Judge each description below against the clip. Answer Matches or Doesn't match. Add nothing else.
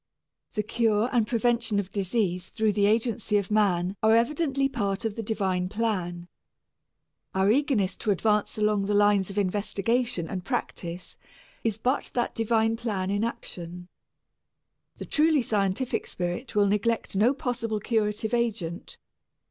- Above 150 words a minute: Doesn't match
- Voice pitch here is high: Matches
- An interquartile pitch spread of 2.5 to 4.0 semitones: Matches